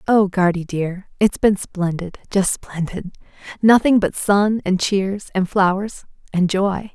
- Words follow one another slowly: Yes, slow, 120 wpm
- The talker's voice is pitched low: No, high, 190 Hz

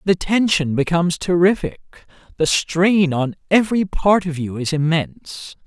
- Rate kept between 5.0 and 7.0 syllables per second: No, 4.6 syllables/s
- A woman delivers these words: No, male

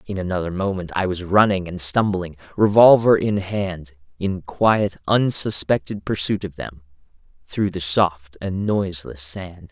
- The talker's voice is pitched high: No, very low, 95 Hz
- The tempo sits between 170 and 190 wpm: No, average, 140 wpm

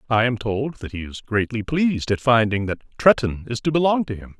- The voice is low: Yes, low, 120 Hz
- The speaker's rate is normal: No, fast, 230 wpm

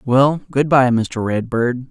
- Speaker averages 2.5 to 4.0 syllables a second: Yes, 3.5 syllables/s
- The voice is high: No, low, 125 Hz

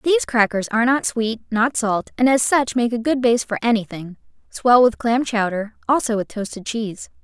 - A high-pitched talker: Yes, high, 235 Hz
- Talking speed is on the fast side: No, average, 190 wpm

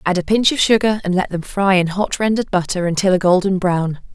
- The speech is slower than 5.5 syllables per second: No, 5.9 syllables/s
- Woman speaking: Yes, female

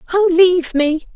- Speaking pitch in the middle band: No, very high, 345 Hz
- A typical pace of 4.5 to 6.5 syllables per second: Yes, 5.1 syllables/s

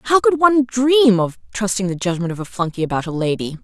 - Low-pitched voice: No, high, 215 Hz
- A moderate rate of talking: No, fast, 230 wpm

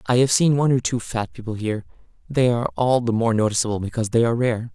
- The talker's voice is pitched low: Yes, low, 120 Hz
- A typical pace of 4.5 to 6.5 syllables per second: No, 7.0 syllables/s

